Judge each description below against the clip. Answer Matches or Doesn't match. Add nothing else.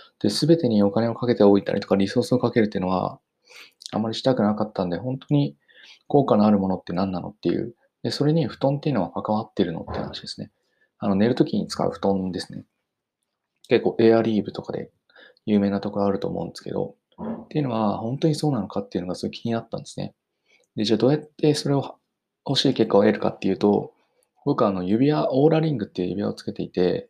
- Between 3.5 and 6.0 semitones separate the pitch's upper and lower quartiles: Matches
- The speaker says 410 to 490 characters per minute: Matches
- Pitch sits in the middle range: Doesn't match